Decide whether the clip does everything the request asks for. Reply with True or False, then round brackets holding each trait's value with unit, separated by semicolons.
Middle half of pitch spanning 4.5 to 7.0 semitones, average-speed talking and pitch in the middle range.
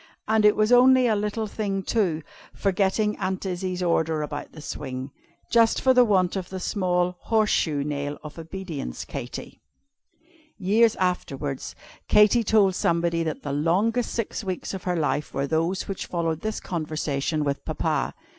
True (5.0 semitones; 155 wpm; 180 Hz)